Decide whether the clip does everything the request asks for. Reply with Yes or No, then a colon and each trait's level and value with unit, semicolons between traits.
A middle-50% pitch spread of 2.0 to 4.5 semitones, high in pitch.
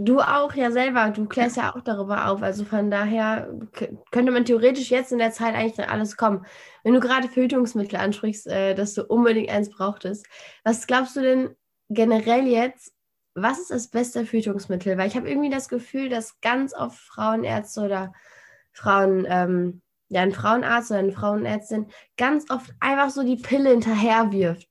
Yes: average, 3.4 semitones; high, 225 Hz